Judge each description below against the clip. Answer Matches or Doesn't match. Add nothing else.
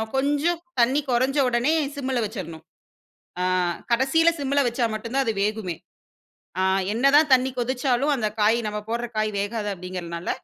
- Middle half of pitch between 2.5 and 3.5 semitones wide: Doesn't match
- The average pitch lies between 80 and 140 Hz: Doesn't match